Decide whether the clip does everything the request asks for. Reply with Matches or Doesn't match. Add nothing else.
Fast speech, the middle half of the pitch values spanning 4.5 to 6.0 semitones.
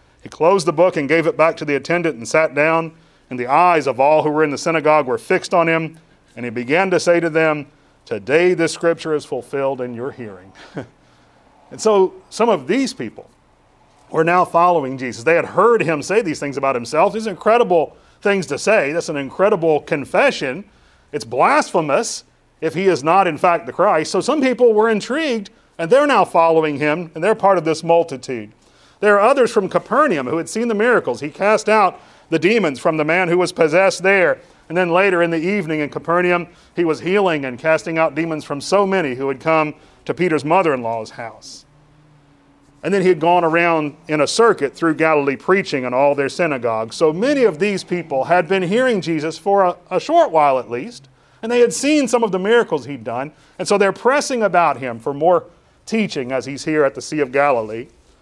Matches